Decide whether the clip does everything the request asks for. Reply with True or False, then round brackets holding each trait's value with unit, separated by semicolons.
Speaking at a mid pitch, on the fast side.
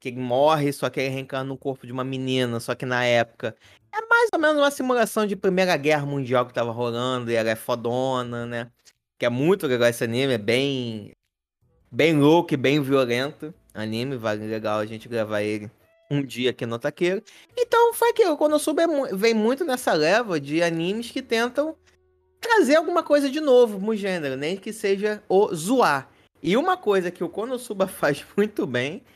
True (145 Hz; 190 wpm)